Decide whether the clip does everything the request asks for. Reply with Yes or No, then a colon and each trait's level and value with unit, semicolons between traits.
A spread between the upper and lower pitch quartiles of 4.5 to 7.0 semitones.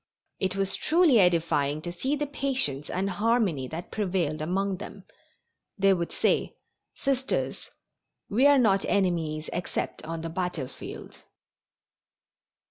Yes: wide, 5.5 semitones